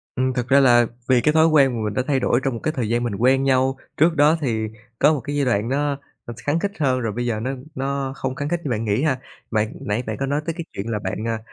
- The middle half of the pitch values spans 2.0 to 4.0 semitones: Yes, average, 3.7 semitones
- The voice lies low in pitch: Yes, low, 130 Hz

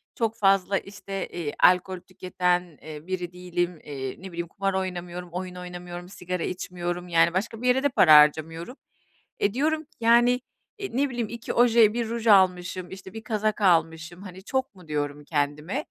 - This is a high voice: No, medium, 180 Hz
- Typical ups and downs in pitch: Yes, average, 3.8 semitones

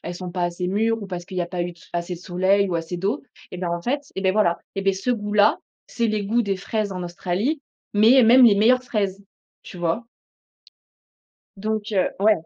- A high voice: Yes, high, 195 Hz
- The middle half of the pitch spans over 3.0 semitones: Yes, average, 3.5 semitones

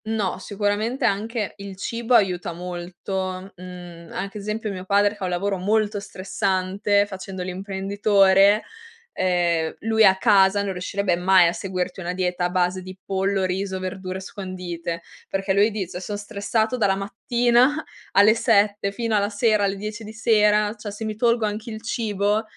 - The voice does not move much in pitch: Yes, narrow, 2.2 semitones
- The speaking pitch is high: Yes, high, 200 Hz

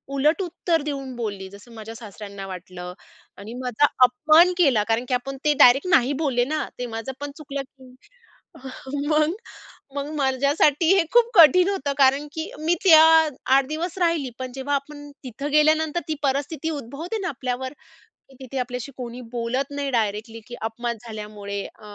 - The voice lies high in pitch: Yes, very high, 270 Hz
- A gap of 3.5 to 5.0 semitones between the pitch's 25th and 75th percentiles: Yes, average, 4.1 semitones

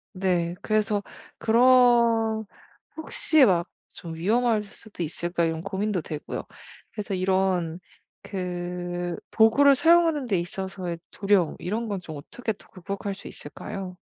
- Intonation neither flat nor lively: Yes, average, 4.1 semitones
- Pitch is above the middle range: Yes, high, 195 Hz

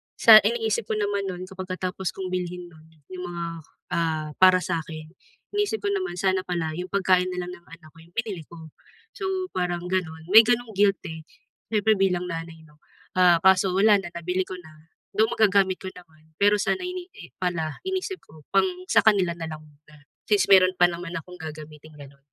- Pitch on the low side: No, medium, 180 Hz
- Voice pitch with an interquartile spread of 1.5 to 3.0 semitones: No, average, 3.6 semitones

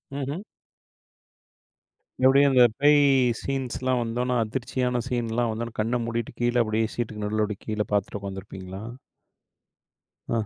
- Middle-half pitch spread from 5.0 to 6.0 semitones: No, average, 2.8 semitones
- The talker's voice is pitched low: Yes, low, 120 Hz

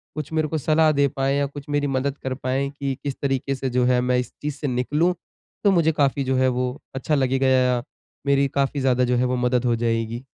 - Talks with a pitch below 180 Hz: Yes, low, 135 Hz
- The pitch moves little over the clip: Yes, narrow, 2.1 semitones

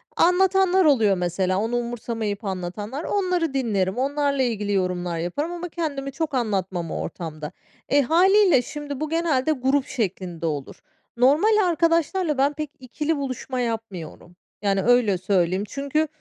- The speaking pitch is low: No, very high, 255 Hz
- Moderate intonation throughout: No, wide, 7.9 semitones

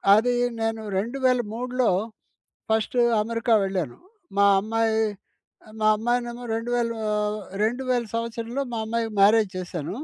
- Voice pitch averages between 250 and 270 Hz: No, high, 230 Hz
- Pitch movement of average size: No, narrow, 1.9 semitones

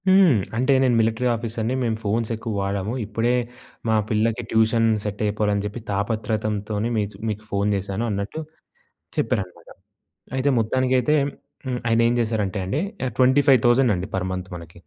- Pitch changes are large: No, average, 2.9 semitones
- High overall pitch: No, low, 110 Hz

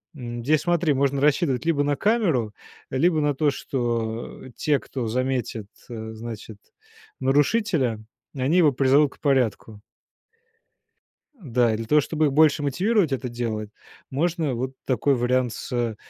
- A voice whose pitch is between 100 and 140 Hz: Yes, low, 135 Hz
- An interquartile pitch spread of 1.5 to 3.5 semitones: No, average, 4.2 semitones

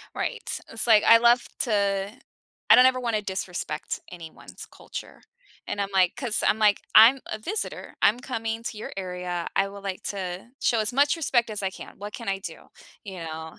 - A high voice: Yes, high, 210 Hz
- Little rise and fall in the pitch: No, average, 3.5 semitones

